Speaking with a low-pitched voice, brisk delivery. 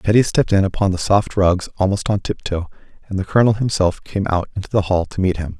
Yes: very low, 95 Hz; fast, 235 wpm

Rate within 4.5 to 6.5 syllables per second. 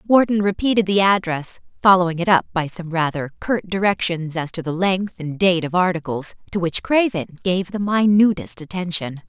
Yes: 5.1 syllables/s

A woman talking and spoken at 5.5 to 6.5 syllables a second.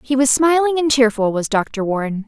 No: female; 5.1 syllables/s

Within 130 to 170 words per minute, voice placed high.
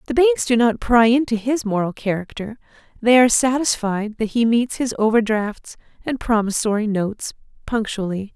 Yes: average, 150 wpm; high, 225 Hz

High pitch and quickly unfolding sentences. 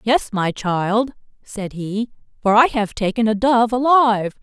No: high, 220 Hz; average, 165 wpm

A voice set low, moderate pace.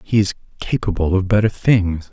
Yes: low, 100 Hz; average, 170 wpm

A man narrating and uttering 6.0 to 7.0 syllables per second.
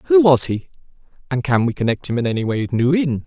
Yes: male; 6.1 syllables/s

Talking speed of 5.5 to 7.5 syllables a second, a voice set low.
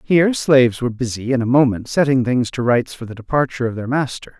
Yes: 6.3 syllables/s; low, 130 Hz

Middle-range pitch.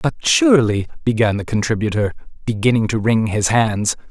No: low, 115 Hz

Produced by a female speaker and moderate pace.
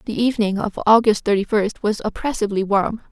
Yes: female; average, 175 wpm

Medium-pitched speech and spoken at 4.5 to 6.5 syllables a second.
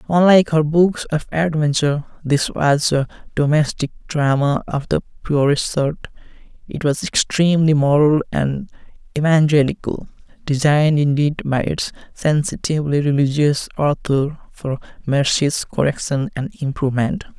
Yes: medium, 145 Hz; 4.6 syllables/s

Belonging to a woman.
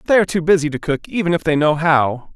No: male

